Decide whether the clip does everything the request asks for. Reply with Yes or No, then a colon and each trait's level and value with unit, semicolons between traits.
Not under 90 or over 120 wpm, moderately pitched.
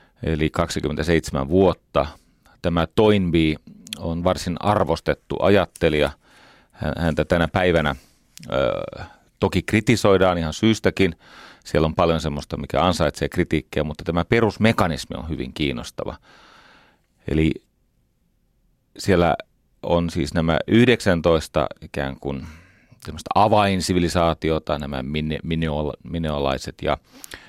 No: average, 100 wpm; very low, 85 Hz